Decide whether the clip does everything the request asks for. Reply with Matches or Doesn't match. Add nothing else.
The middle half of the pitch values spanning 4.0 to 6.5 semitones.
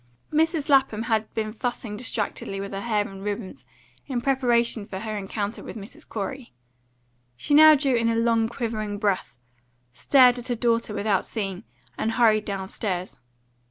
Doesn't match